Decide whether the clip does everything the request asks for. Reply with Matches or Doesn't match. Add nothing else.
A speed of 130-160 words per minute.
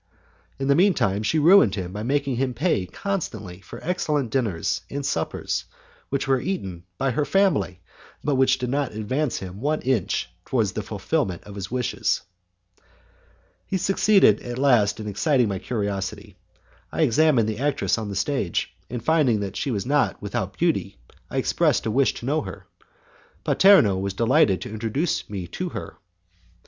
Doesn't match